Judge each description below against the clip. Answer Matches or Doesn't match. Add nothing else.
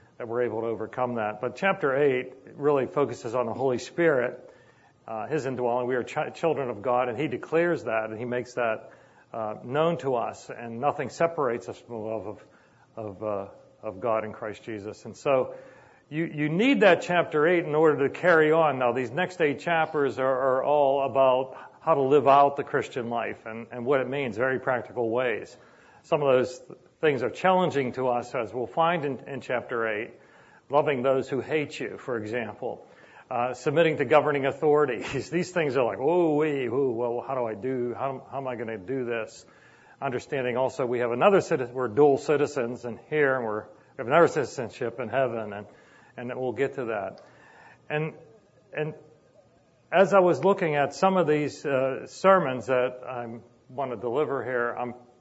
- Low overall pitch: Matches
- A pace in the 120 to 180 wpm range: Doesn't match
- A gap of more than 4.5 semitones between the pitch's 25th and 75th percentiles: Doesn't match